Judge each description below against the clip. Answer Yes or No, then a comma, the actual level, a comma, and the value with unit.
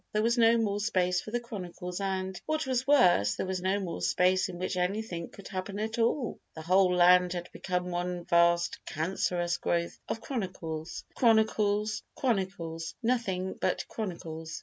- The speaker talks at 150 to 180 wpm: Yes, average, 165 wpm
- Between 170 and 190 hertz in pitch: Yes, medium, 185 Hz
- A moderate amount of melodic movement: Yes, average, 3.6 semitones